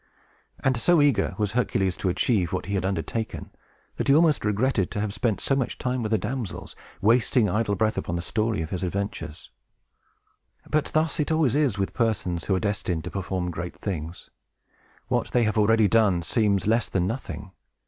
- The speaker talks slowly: No, average, 190 wpm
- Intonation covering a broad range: No, average, 4.2 semitones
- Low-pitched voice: Yes, low, 105 Hz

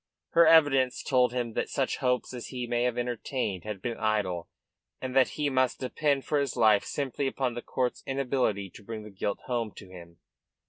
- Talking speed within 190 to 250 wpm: Yes, average, 195 wpm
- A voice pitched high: No, low, 125 Hz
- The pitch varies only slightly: No, average, 3.6 semitones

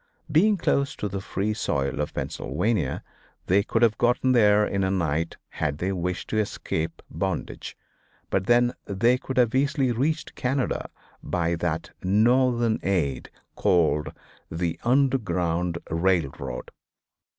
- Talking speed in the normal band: No, slow, 130 wpm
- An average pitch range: No, wide, 6.3 semitones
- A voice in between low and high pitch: No, low, 100 Hz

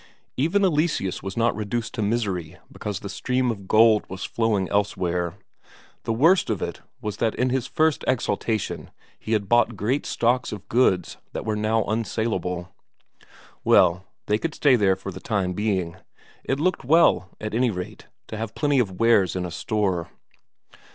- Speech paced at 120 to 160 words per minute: No, average, 170 wpm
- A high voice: No, low, 110 Hz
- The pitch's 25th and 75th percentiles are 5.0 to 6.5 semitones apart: No, average, 4.2 semitones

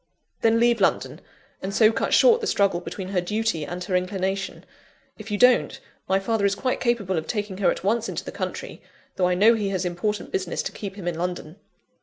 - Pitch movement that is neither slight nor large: Yes, average, 3.4 semitones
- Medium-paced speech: No, fast, 215 wpm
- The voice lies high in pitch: Yes, high, 195 Hz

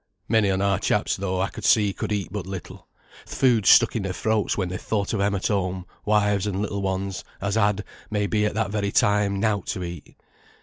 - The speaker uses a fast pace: Yes, fast, 225 wpm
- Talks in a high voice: No, low, 100 Hz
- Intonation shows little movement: Yes, narrow, 1.5 semitones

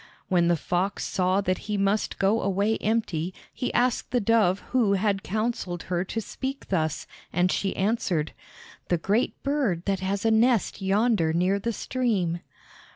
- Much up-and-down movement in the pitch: No, average, 3.7 semitones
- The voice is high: Yes, high, 200 Hz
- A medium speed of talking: Yes, average, 160 wpm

